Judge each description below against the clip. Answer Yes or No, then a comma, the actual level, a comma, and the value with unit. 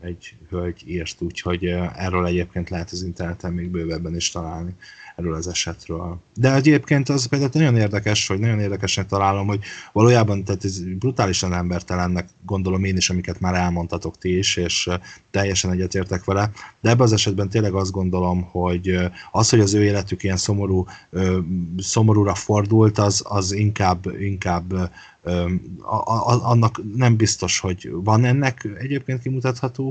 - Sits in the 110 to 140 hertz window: No, very low, 95 Hz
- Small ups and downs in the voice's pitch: No, average, 3.3 semitones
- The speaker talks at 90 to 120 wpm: No, average, 150 wpm